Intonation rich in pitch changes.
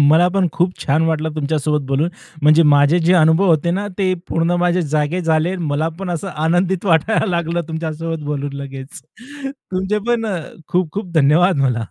No: average, 3.1 semitones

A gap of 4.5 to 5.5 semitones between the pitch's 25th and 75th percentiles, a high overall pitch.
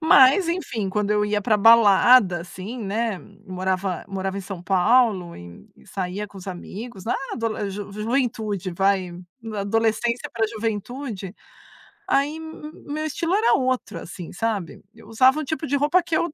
Yes: average, 4.8 semitones; high, 215 Hz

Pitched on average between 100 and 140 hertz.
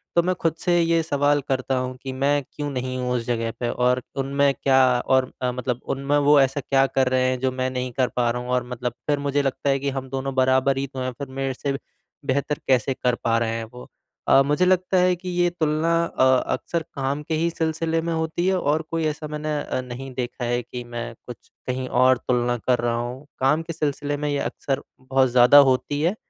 Yes: low, 135 Hz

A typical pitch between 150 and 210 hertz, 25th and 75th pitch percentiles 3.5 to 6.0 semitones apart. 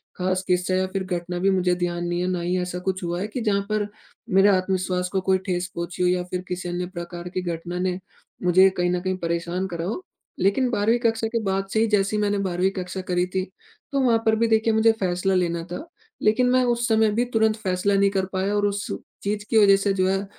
No: high, 190 Hz; narrow, 2.6 semitones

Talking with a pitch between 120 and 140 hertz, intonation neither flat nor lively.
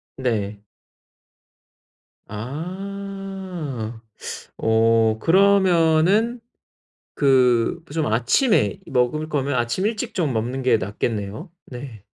No: low, 135 Hz; wide, 8.6 semitones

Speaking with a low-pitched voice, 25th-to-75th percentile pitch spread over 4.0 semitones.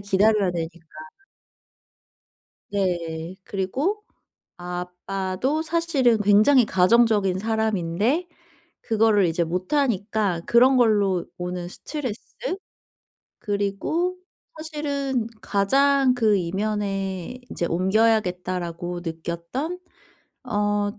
No: high, 205 Hz; wide, 5.4 semitones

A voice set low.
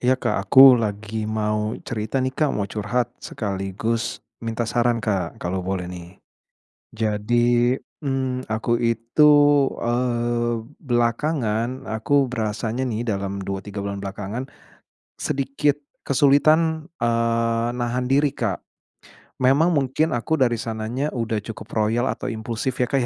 Yes: low, 115 Hz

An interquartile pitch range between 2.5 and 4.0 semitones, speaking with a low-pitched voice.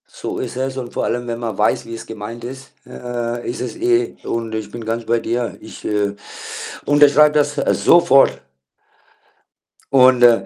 Yes: average, 2.8 semitones; low, 120 Hz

